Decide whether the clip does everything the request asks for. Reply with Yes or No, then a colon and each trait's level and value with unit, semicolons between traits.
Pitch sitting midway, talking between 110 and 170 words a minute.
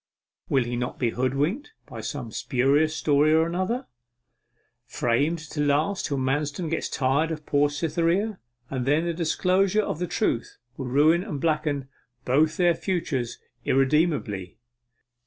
Yes: medium, 150 Hz; average, 140 wpm